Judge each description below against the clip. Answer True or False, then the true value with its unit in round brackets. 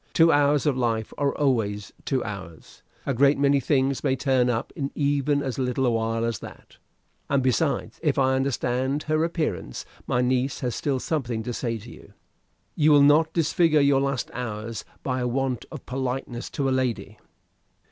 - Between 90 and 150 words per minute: False (180 wpm)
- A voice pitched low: True (130 Hz)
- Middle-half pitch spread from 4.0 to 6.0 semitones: False (2.7 semitones)